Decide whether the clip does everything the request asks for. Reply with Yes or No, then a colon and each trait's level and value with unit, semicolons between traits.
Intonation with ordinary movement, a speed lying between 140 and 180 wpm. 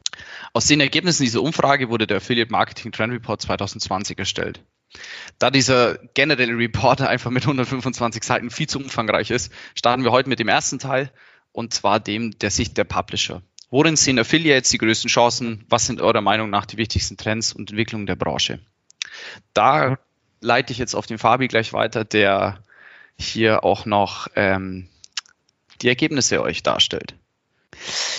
Yes: average, 3.3 semitones; average, 165 wpm